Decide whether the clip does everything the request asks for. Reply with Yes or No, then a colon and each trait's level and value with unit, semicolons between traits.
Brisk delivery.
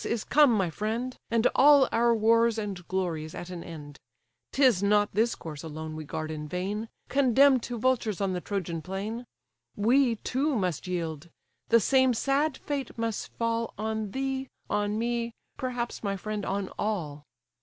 No: average, 165 wpm